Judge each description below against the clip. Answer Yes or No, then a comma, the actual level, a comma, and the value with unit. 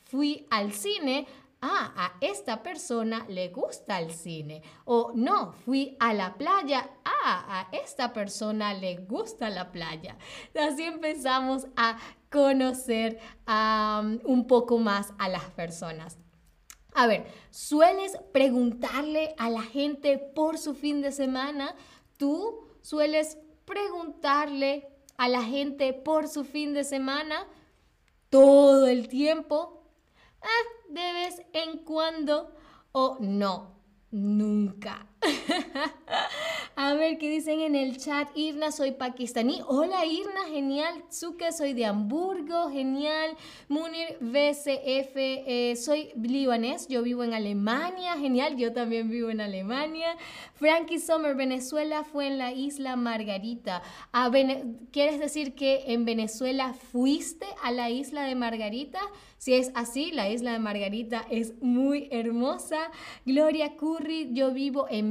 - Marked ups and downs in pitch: No, average, 4.6 semitones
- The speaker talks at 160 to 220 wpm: No, slow, 125 wpm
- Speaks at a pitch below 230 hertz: No, very high, 270 Hz